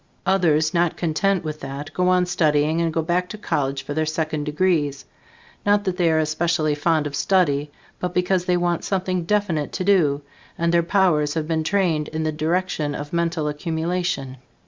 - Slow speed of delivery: No, average, 185 wpm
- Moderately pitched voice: Yes, medium, 165 Hz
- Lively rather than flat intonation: No, average, 3.0 semitones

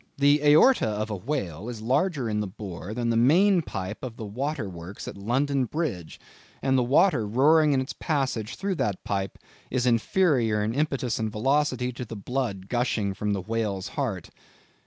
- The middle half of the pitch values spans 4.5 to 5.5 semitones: Yes, average, 5.2 semitones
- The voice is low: Yes, low, 120 Hz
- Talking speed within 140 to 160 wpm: No, average, 180 wpm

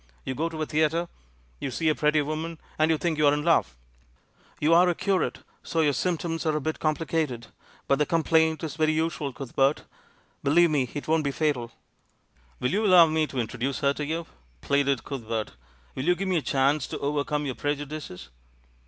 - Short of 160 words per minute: No, average, 190 wpm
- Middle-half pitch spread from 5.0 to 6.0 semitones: No, average, 2.7 semitones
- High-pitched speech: No, medium, 155 Hz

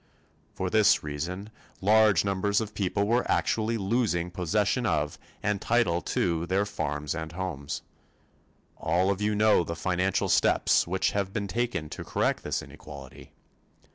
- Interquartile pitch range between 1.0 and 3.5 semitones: No, average, 3.9 semitones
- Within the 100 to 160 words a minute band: Yes, average, 145 wpm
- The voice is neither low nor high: No, very low, 95 Hz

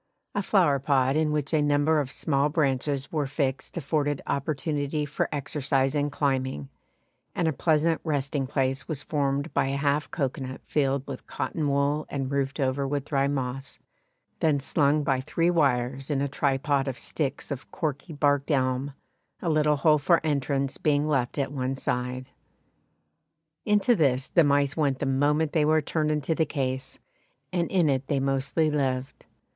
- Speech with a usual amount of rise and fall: No, narrow, 2.1 semitones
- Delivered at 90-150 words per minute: No, average, 165 wpm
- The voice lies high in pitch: No, medium, 140 Hz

